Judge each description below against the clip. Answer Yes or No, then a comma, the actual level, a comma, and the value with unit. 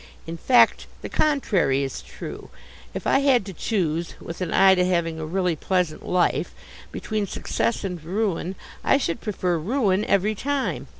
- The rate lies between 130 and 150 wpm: No, average, 165 wpm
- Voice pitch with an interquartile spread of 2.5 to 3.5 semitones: No, average, 4.4 semitones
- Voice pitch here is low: No, medium, 185 Hz